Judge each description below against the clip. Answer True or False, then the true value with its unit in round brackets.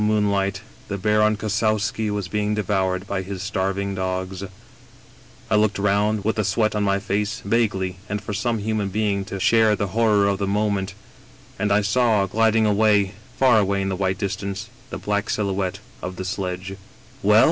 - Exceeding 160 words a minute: True (180 wpm)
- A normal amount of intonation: False (1.7 semitones)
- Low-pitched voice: True (100 Hz)